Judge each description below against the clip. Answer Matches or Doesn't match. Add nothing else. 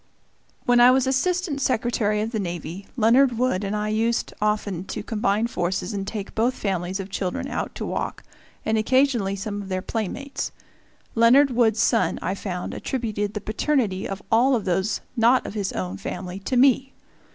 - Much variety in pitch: Doesn't match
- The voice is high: Matches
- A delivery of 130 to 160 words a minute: Doesn't match